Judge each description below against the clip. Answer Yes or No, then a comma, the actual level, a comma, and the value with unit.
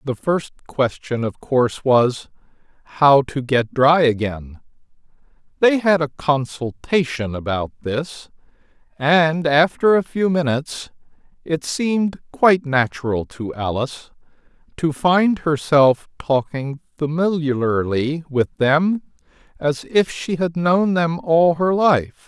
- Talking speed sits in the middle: No, slow, 120 wpm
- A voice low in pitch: No, medium, 150 Hz